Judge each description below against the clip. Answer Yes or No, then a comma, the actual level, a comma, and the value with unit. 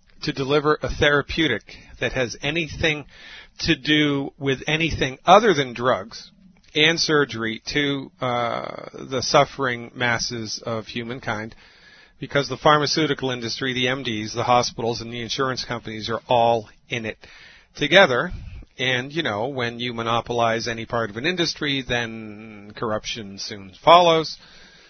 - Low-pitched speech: Yes, low, 125 Hz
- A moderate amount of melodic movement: Yes, average, 4.1 semitones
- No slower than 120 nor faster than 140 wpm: Yes, slow, 135 wpm